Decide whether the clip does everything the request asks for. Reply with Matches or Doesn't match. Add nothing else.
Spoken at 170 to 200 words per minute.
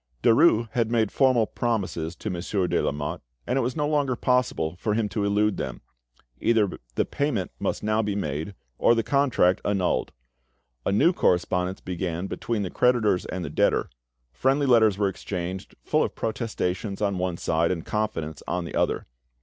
Matches